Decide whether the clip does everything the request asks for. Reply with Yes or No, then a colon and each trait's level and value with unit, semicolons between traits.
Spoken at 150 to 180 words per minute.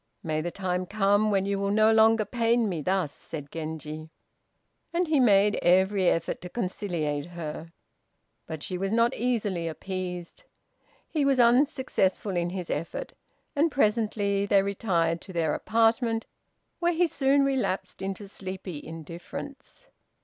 No: average, 140 wpm